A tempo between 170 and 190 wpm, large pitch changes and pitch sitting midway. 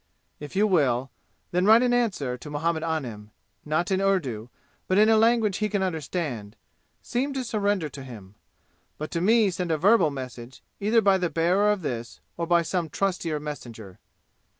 Yes: average, 175 wpm; wide, 6.6 semitones; medium, 170 Hz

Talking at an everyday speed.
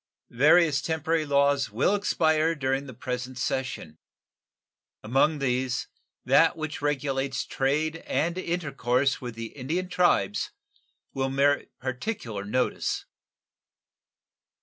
No: slow, 105 wpm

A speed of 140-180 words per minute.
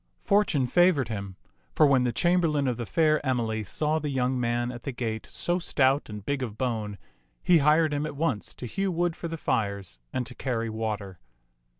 No: average, 200 wpm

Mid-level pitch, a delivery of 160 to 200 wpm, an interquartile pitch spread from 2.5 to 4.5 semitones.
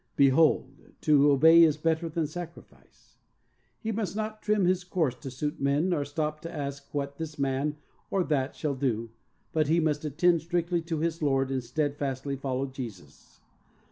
Yes: medium, 150 Hz; average, 170 wpm; average, 3.3 semitones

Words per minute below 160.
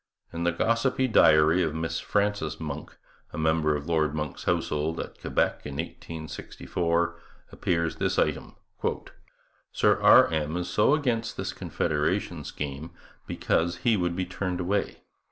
Yes: average, 140 wpm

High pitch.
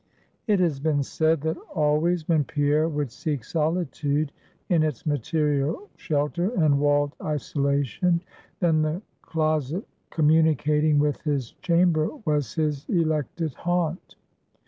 No: medium, 155 Hz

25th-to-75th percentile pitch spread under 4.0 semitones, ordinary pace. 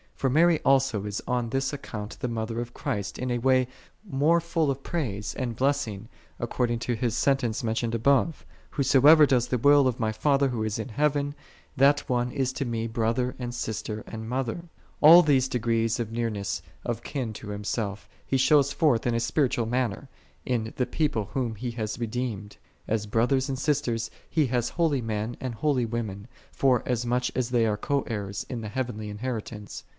Yes: average, 3.3 semitones; average, 185 wpm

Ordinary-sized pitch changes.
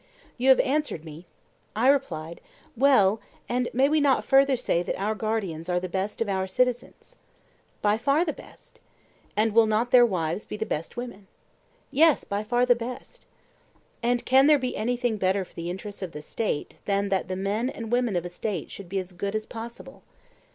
Yes: average, 4.8 semitones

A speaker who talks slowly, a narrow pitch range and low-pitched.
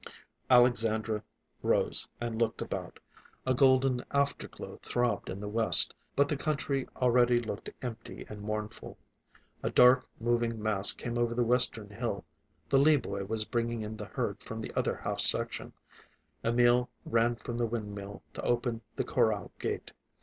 No: average, 155 wpm; narrow, 2.2 semitones; low, 120 Hz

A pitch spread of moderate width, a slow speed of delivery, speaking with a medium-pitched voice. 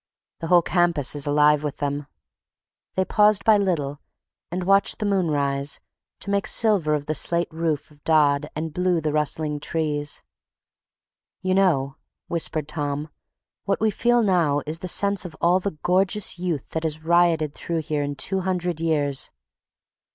No: average, 3.7 semitones; average, 165 wpm; medium, 160 Hz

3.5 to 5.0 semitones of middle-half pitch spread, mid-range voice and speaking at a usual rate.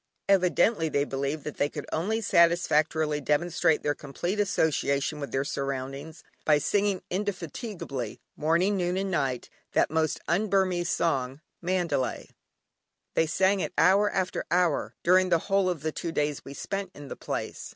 Yes: average, 4.1 semitones; medium, 165 Hz; average, 155 wpm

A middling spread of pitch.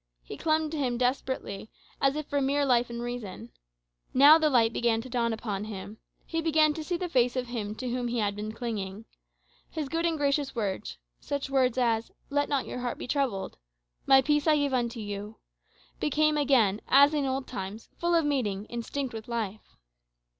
Yes: average, 4.3 semitones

